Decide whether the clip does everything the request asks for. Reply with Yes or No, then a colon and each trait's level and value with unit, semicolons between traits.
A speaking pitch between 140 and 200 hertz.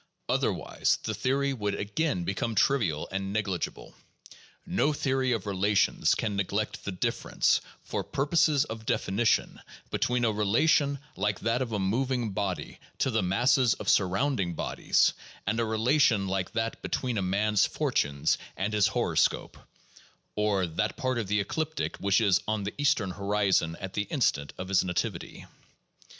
No: low, 105 Hz